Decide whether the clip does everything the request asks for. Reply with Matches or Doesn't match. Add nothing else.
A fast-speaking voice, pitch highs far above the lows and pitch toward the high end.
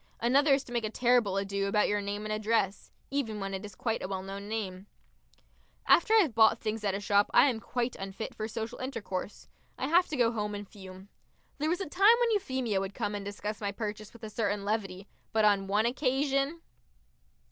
Doesn't match